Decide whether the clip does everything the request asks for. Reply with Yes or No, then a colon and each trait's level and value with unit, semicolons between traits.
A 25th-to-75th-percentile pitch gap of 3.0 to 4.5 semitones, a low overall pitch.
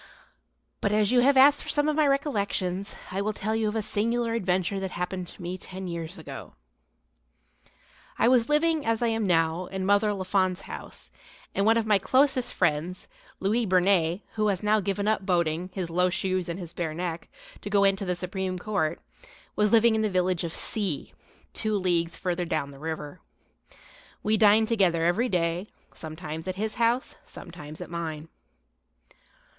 No: average, 3.7 semitones; high, 190 Hz